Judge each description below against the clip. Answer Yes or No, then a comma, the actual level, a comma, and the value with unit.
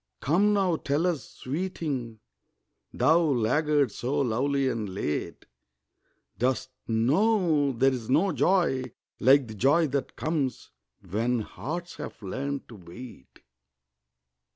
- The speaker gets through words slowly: Yes, slow, 110 wpm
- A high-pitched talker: No, low, 135 Hz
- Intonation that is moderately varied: Yes, average, 4.9 semitones